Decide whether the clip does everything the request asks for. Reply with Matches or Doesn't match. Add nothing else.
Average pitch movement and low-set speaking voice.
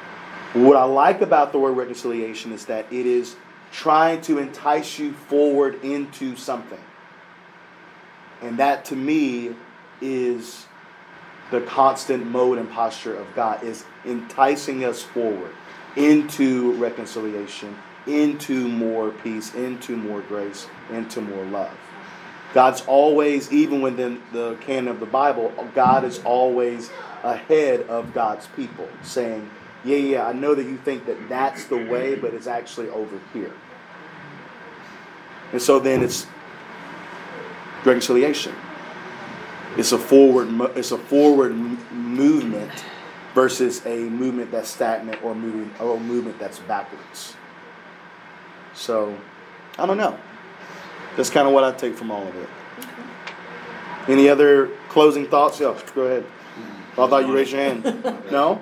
Matches